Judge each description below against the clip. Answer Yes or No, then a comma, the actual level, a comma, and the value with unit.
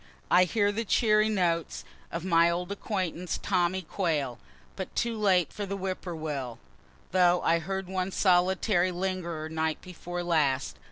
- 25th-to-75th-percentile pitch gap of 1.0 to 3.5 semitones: Yes, narrow, 2.4 semitones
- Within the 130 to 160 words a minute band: Yes, average, 155 wpm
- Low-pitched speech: No, medium, 180 Hz